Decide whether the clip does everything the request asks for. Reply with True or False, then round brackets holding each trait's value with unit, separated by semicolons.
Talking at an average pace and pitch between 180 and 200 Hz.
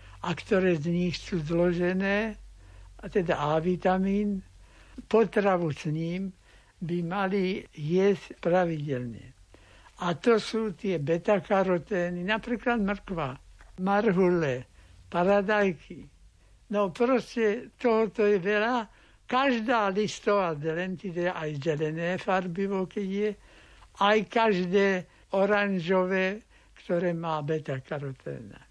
False (95 wpm; 185 Hz)